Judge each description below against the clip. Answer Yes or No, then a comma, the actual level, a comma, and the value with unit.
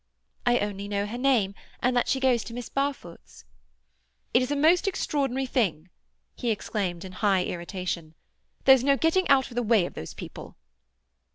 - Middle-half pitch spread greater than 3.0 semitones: Yes, wide, 5.4 semitones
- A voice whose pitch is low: No, high, 240 Hz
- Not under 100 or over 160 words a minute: No, average, 170 wpm